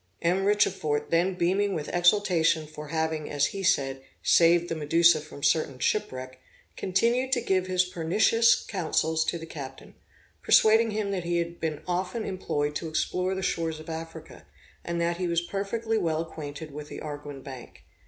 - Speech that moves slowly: No, average, 165 wpm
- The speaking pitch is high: No, medium, 170 Hz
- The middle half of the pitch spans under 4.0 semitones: Yes, average, 3.5 semitones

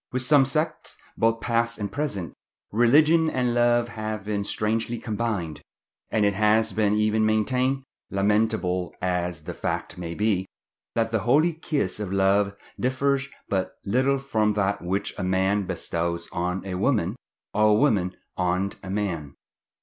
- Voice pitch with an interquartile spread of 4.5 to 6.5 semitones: No, average, 3.9 semitones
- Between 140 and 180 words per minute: Yes, average, 150 wpm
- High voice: No, low, 105 Hz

